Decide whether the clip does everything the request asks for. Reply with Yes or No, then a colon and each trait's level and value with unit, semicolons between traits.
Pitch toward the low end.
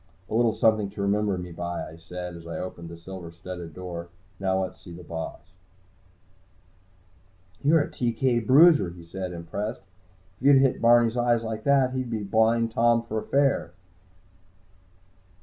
Yes: low, 105 Hz